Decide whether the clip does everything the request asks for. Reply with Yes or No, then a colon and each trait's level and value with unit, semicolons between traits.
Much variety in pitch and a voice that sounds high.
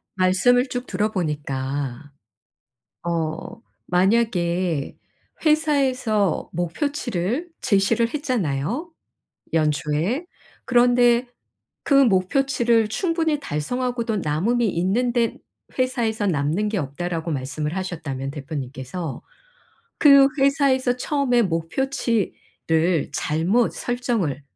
Yes: wide, 7.5 semitones; high, 205 Hz